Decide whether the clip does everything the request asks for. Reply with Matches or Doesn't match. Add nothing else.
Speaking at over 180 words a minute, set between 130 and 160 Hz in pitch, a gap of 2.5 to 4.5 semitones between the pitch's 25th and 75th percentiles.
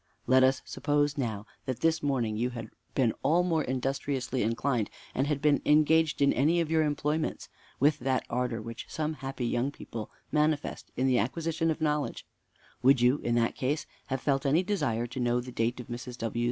Matches